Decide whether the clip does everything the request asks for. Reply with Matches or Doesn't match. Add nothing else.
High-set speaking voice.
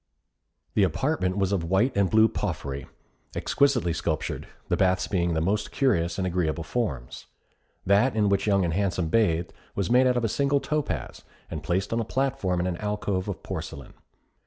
Doesn't match